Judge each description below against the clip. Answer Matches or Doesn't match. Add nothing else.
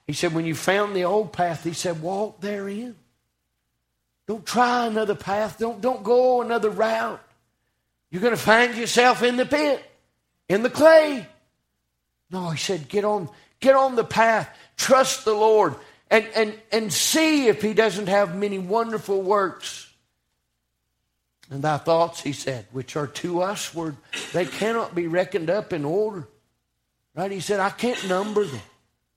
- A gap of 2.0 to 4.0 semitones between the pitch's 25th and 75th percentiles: Doesn't match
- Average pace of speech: Matches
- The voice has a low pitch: Doesn't match